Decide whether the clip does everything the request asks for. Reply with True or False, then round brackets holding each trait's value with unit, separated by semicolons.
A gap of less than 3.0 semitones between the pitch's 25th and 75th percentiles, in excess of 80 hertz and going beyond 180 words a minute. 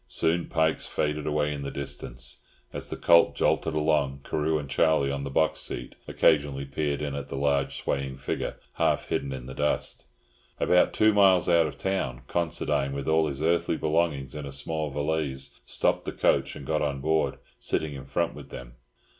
False (2.5 semitones; 75 Hz; 190 wpm)